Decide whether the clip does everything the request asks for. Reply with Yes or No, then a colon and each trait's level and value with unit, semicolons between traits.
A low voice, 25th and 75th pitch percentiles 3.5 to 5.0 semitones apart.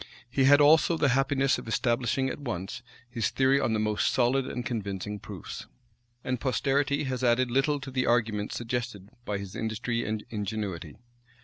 Yes: low, 120 Hz; average, 3.9 semitones